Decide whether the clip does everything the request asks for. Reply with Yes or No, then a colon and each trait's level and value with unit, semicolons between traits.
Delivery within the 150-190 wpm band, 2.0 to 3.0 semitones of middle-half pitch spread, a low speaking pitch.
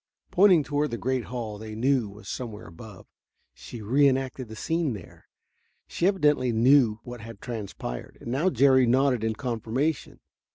No: average, 155 wpm; average, 3.9 semitones; low, 125 Hz